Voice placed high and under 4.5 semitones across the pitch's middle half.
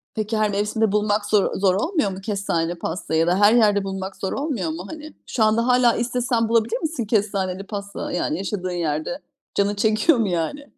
Yes: high, 205 Hz; average, 3.5 semitones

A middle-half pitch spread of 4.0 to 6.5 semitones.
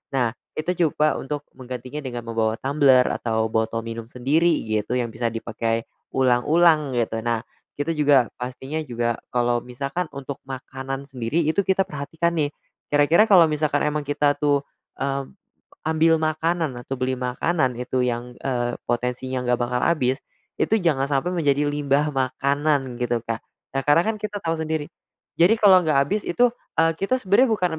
Yes: average, 4.3 semitones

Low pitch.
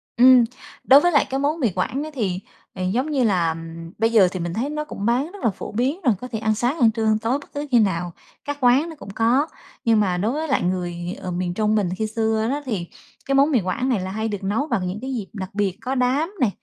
No: high, 225 Hz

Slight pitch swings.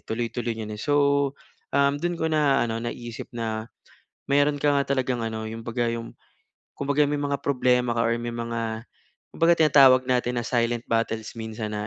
No: average, 3.6 semitones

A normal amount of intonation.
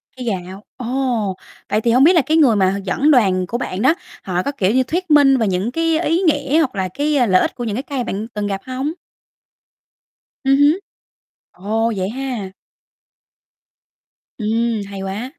No: wide, 5.9 semitones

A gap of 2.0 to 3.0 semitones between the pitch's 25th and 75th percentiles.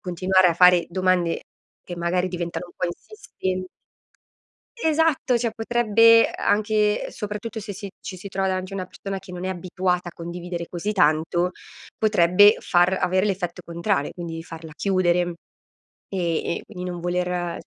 Yes: average, 2.7 semitones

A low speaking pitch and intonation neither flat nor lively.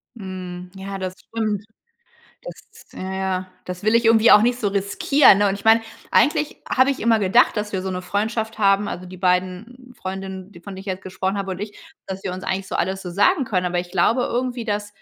No: high, 195 Hz; average, 3.1 semitones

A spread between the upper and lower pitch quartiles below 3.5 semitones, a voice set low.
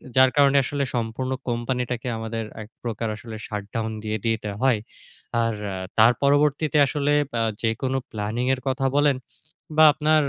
No: average, 3.8 semitones; low, 125 Hz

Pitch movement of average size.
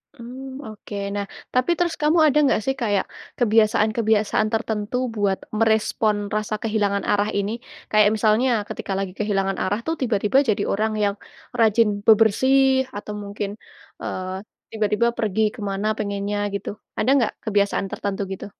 No: narrow, 2.2 semitones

